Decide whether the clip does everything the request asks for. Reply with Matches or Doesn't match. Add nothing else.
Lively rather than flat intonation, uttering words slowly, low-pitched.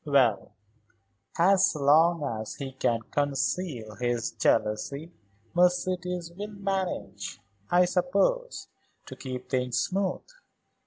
Doesn't match